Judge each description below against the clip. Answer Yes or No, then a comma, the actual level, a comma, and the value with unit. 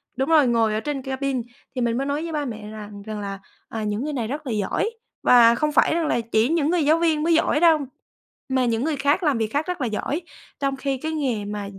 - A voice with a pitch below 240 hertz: No, very high, 265 Hz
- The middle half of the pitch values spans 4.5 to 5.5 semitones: Yes, average, 5.2 semitones